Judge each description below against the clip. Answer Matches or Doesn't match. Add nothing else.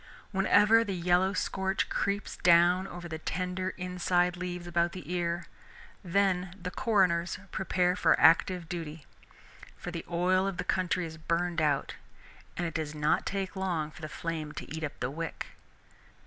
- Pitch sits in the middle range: Matches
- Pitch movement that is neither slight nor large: Doesn't match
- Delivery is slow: Doesn't match